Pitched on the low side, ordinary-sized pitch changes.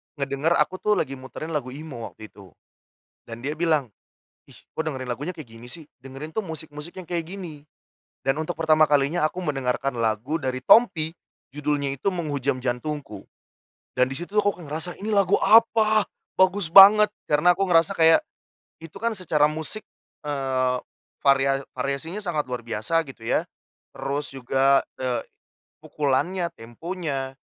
No: medium, 150 Hz; average, 4.5 semitones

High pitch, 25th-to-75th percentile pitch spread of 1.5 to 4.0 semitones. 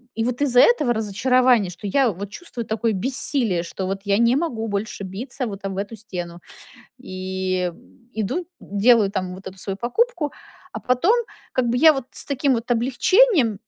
No: high, 225 Hz; average, 4.7 semitones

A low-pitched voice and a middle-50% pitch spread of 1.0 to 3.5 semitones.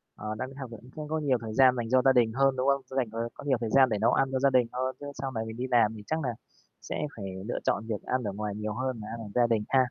Yes: low, 125 Hz; average, 2.9 semitones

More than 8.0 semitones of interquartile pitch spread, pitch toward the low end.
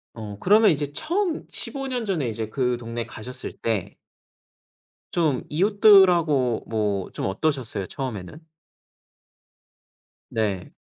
Yes: wide, 9.0 semitones; low, 130 Hz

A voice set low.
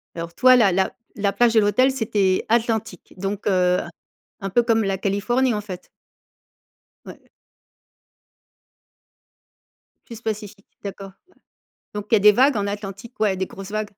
No: high, 205 Hz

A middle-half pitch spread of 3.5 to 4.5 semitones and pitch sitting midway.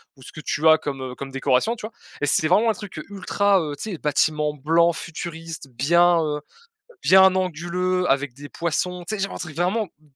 Yes: average, 3.9 semitones; medium, 165 Hz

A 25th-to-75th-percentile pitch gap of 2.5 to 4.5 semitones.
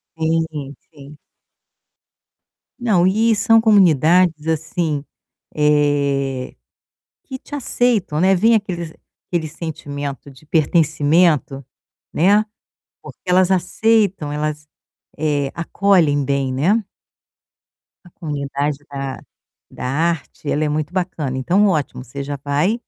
Yes: average, 4.2 semitones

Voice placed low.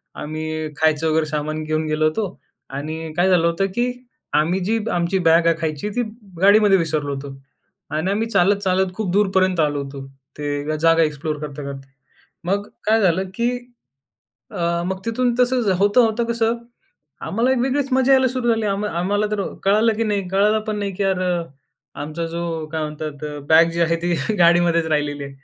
No: medium, 175 Hz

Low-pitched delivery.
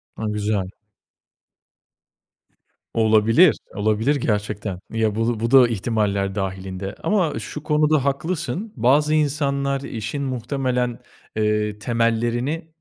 Yes: low, 115 Hz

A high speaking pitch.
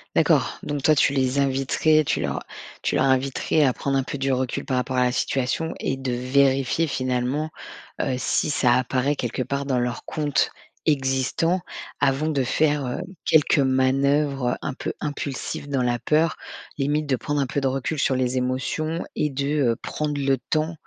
No: low, 135 Hz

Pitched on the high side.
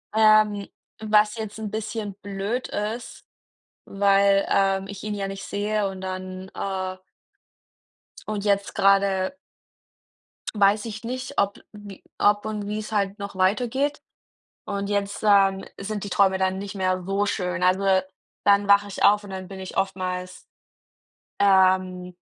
Yes: high, 200 Hz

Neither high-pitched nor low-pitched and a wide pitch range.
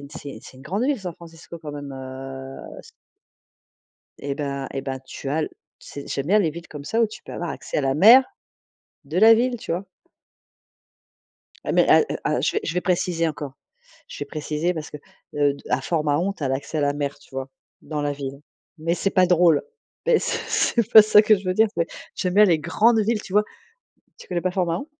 Yes: medium, 165 Hz; wide, 5.8 semitones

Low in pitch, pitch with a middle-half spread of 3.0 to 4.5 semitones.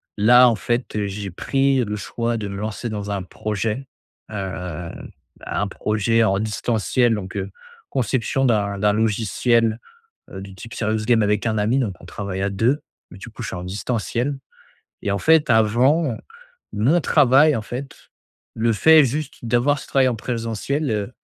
Yes: low, 110 Hz; average, 3.5 semitones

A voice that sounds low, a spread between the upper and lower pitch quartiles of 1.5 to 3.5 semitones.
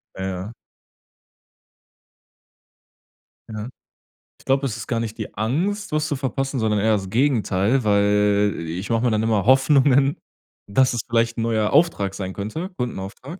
No: low, 115 Hz; average, 4.6 semitones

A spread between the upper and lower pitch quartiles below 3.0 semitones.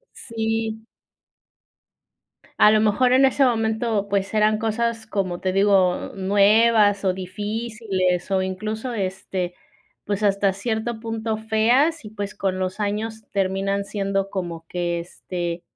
Yes: narrow, 2.6 semitones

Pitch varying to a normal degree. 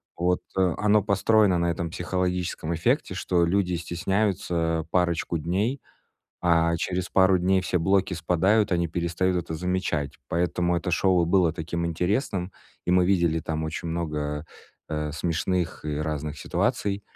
No: narrow, 2.1 semitones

